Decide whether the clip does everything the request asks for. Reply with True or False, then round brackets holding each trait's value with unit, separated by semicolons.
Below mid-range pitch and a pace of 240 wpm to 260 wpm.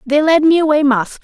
False (290 Hz; 245 wpm)